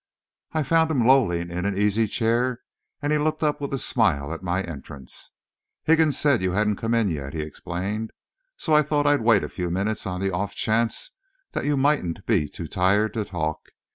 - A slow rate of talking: No, average, 200 wpm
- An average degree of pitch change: No, wide, 7.1 semitones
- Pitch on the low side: Yes, low, 105 Hz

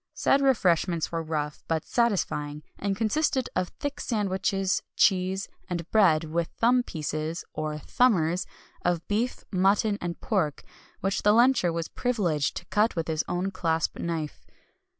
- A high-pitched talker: No, medium, 180 Hz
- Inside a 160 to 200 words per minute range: No, average, 145 wpm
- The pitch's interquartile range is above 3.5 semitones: Yes, average, 4.6 semitones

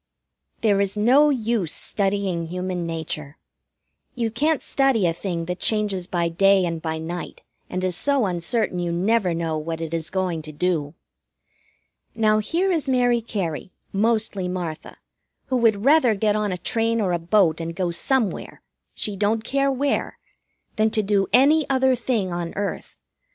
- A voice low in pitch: No, high, 200 Hz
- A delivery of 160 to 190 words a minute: Yes, average, 165 wpm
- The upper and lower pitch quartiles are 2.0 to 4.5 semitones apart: No, average, 5.1 semitones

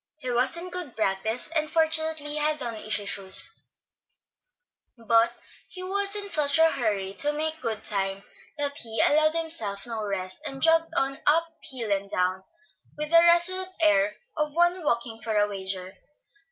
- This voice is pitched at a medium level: No, very high, 285 Hz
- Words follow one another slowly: No, average, 165 wpm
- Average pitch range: No, wide, 7.1 semitones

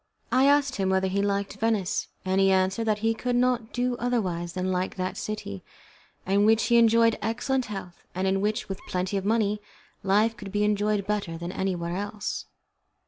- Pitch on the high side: Yes, high, 205 Hz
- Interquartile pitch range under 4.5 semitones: Yes, average, 3.0 semitones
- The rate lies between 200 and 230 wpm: No, average, 190 wpm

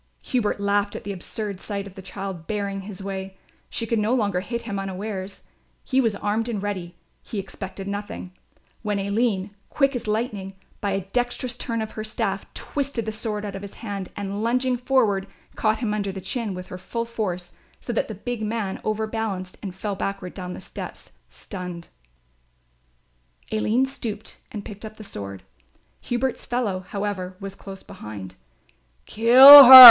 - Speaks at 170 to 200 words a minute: Yes, average, 175 wpm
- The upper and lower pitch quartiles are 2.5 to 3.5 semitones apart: Yes, average, 2.9 semitones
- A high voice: Yes, high, 205 Hz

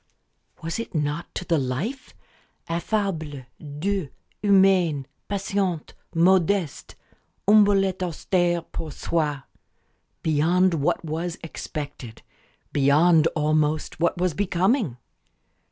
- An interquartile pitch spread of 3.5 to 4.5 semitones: Yes, average, 3.9 semitones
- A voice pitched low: No, medium, 170 Hz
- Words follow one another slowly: Yes, slow, 95 wpm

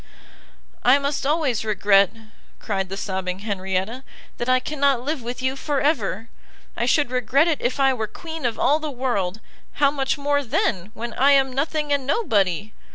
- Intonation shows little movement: No, average, 5.1 semitones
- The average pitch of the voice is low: No, very high, 255 Hz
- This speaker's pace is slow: No, average, 175 wpm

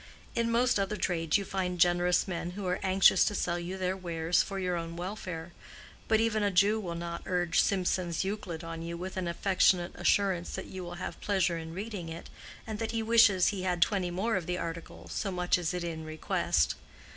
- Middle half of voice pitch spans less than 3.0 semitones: Yes, narrow, 2.5 semitones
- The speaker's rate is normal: No, fast, 210 wpm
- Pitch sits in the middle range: Yes, medium, 180 Hz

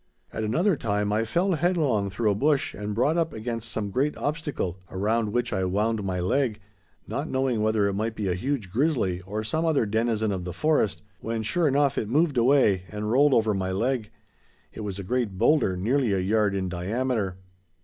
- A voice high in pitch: No, low, 110 Hz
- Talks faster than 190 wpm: Yes, average, 200 wpm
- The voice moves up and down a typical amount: Yes, average, 4.9 semitones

